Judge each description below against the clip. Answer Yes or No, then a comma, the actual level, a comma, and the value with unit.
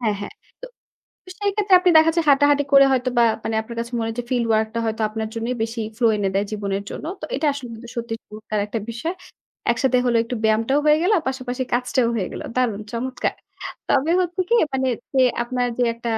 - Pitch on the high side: Yes, high, 240 Hz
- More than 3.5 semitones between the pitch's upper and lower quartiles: No, average, 3.1 semitones